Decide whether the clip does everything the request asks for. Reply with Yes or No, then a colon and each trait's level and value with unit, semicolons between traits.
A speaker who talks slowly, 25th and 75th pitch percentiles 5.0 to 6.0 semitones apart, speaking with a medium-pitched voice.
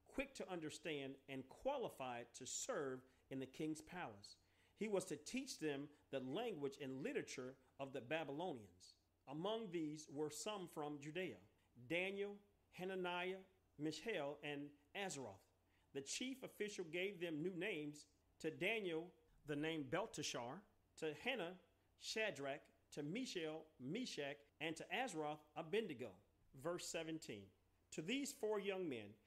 Yes: slow, 130 wpm; average, 5.3 semitones; medium, 150 Hz